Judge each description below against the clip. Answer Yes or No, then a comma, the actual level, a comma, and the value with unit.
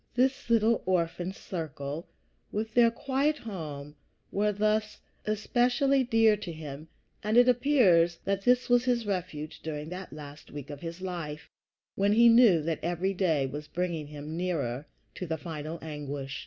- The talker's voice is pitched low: No, medium, 180 Hz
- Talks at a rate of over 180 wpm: No, average, 155 wpm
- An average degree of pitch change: No, wide, 6.6 semitones